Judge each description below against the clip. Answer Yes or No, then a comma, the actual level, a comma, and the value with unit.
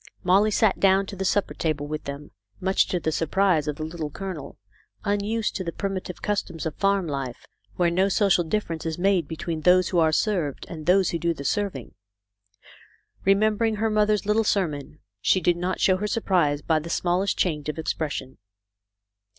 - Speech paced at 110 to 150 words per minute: No, average, 185 wpm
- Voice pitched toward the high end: No, medium, 180 Hz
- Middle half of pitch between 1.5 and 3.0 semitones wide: No, average, 4.0 semitones